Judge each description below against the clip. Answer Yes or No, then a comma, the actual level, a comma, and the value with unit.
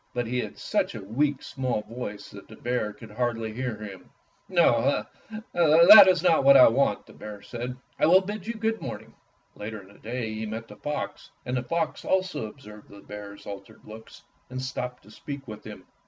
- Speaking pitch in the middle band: No, low, 120 Hz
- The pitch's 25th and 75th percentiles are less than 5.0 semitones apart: No, average, 5.3 semitones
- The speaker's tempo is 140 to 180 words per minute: No, average, 200 wpm